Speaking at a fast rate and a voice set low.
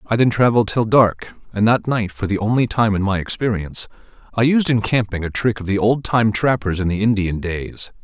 Yes: fast, 225 wpm; low, 110 Hz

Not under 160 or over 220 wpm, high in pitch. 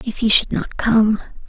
Yes: fast, 205 wpm; high, 220 Hz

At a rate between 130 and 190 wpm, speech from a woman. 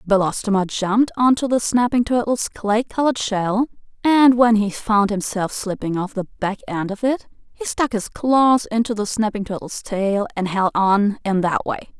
Yes: average, 180 wpm; female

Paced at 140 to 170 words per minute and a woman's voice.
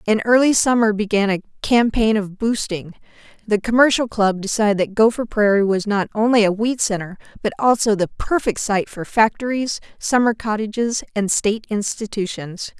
Yes: average, 155 wpm; female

